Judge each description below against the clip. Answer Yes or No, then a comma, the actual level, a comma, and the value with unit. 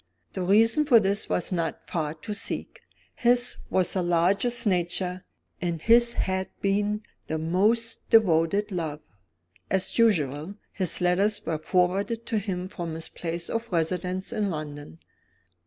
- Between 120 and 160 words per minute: Yes, average, 140 wpm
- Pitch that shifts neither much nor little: Yes, average, 3.9 semitones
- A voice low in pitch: No, medium, 185 Hz